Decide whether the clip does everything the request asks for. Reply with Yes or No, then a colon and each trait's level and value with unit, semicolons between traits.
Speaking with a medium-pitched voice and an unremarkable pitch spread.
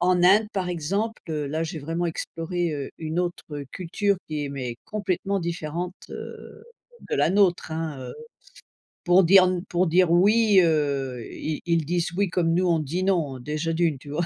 Yes: medium, 170 Hz; average, 3.0 semitones